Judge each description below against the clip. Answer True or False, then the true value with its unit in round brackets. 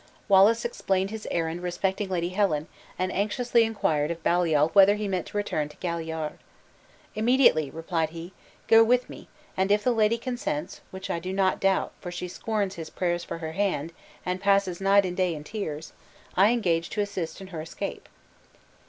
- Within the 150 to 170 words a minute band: False (180 wpm)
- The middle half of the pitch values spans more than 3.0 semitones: True (3.6 semitones)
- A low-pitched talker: False (190 Hz)